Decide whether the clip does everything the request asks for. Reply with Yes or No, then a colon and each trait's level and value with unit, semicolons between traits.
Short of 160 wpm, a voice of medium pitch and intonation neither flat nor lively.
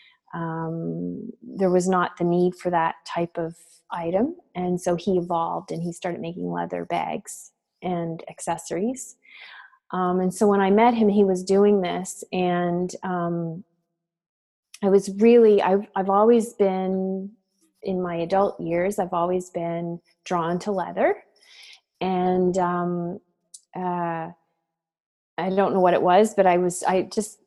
No: average, 150 wpm; medium, 180 Hz; narrow, 2.3 semitones